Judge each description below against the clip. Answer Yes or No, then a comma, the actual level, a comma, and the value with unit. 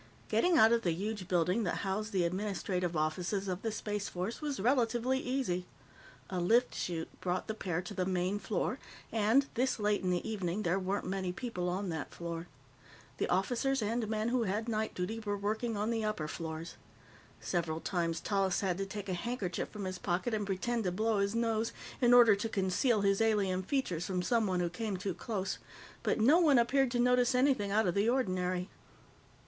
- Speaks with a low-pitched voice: No, high, 205 Hz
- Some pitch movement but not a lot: Yes, average, 4.0 semitones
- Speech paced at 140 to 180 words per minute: No, average, 195 wpm